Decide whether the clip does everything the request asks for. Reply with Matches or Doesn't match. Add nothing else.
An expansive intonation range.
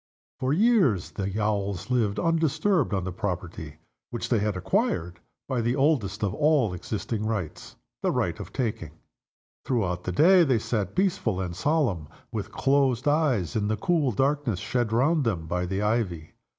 Matches